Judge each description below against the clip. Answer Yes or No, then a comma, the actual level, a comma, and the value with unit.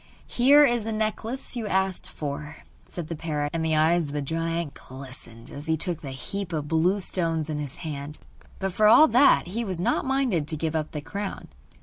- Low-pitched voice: No, medium, 165 Hz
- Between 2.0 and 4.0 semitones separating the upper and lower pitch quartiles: No, average, 5.3 semitones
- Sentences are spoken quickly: Yes, fast, 210 wpm